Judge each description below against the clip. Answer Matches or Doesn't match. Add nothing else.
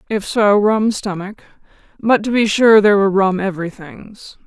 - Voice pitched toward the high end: Matches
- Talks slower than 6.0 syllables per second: Matches